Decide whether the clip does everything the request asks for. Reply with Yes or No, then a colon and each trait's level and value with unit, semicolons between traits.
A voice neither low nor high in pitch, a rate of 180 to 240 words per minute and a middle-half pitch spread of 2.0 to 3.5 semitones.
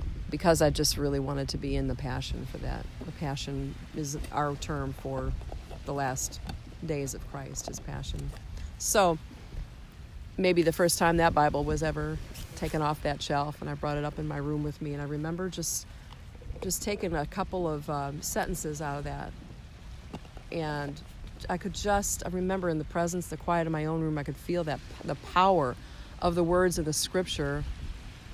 Yes: medium, 150 Hz; average, 190 wpm; average, 3.1 semitones